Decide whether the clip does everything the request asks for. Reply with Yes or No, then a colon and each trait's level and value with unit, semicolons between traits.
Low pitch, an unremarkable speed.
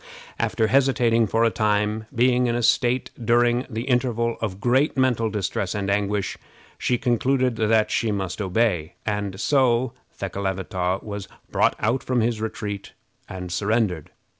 Yes: low, 110 Hz; average, 145 wpm